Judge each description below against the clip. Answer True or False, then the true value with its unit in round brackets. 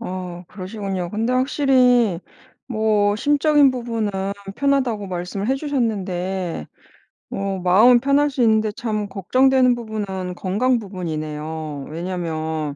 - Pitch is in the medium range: False (205 Hz)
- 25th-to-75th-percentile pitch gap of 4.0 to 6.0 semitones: True (5.5 semitones)